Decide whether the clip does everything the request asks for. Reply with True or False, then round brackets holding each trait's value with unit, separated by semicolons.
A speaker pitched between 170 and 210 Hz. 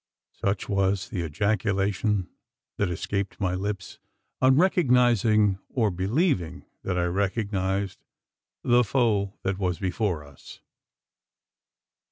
False (100 Hz)